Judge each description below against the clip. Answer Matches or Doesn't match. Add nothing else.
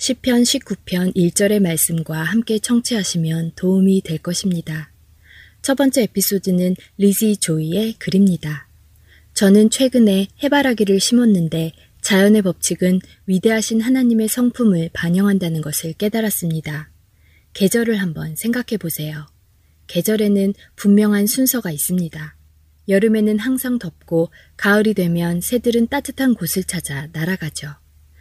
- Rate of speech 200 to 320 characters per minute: Matches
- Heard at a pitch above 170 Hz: Matches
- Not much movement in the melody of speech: Doesn't match